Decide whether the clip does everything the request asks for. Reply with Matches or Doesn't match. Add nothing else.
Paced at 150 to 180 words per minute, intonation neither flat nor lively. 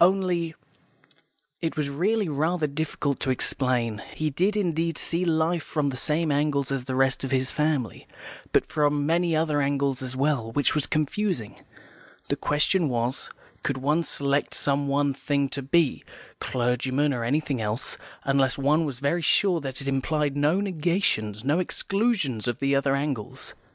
Matches